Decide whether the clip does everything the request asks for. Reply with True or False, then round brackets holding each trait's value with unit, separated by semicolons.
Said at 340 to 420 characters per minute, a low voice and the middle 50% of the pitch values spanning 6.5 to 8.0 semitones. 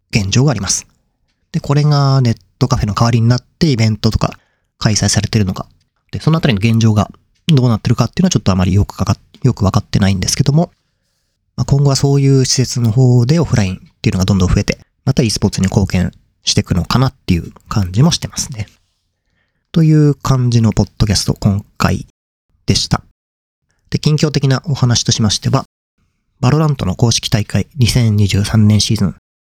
False (395 characters per minute; 115 Hz; 5.3 semitones)